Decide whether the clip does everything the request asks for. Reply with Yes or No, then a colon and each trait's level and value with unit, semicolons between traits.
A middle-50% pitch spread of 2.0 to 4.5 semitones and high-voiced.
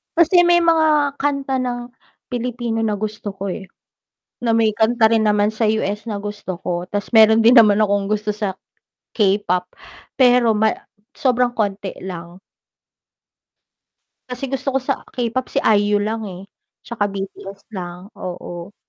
Yes: average, 3.5 semitones; high, 215 Hz